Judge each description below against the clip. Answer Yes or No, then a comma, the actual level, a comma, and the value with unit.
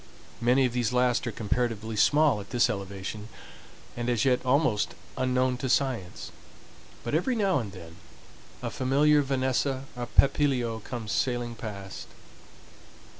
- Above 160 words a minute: No, slow, 135 wpm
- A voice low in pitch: Yes, low, 125 Hz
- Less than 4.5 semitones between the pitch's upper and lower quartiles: Yes, average, 3.1 semitones